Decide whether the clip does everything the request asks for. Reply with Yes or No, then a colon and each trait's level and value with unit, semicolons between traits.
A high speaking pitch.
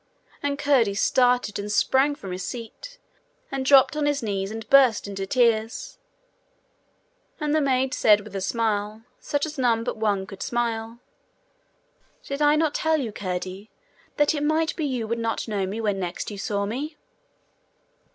Yes: high, 230 Hz